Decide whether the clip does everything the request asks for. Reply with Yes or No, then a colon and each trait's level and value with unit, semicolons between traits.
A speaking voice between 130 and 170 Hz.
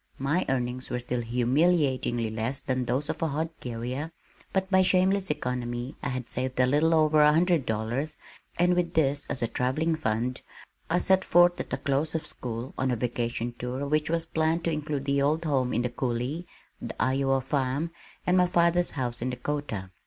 Yes: medium, 140 Hz